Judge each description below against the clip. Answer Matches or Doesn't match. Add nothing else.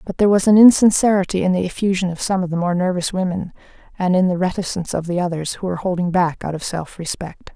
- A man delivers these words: Doesn't match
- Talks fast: Matches